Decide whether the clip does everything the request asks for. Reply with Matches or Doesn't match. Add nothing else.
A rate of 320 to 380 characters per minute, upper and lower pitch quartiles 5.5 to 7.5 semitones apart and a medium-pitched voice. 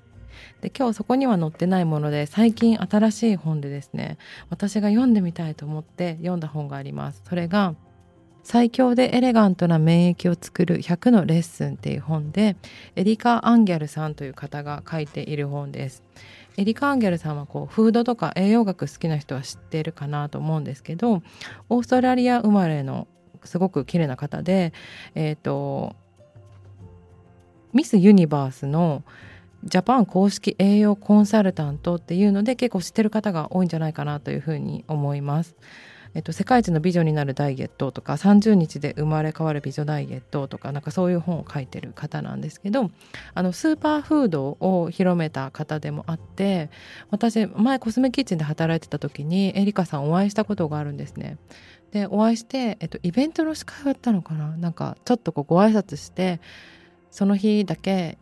Matches